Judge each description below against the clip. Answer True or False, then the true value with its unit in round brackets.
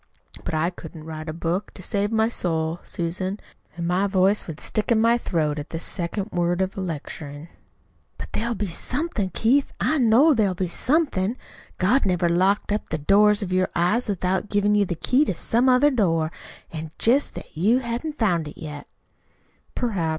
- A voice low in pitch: False (190 Hz)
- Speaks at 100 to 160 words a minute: False (185 wpm)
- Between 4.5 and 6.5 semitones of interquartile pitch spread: True (4.9 semitones)